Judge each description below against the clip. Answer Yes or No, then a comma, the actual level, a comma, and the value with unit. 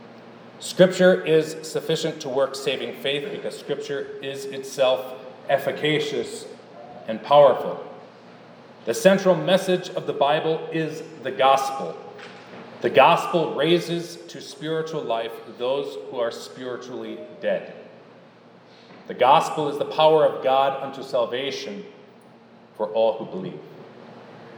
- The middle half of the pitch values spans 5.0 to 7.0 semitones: Yes, average, 5.3 semitones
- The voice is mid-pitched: Yes, medium, 155 Hz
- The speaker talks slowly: Yes, slow, 115 wpm